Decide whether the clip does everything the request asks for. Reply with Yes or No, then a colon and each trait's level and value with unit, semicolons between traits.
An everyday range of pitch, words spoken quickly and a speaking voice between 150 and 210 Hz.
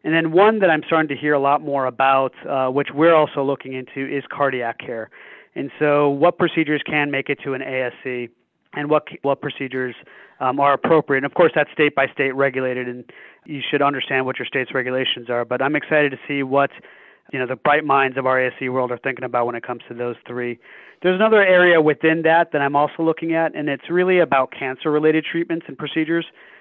No: average, 3.2 semitones; fast, 215 wpm; medium, 140 Hz